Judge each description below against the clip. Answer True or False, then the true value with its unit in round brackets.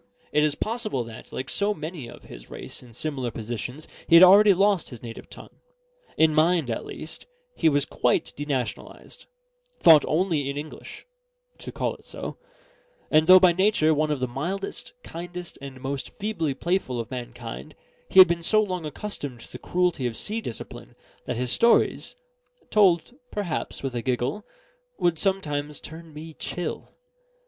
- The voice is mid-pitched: True (155 Hz)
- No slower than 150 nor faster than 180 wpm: True (165 wpm)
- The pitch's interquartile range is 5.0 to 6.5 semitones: True (5.6 semitones)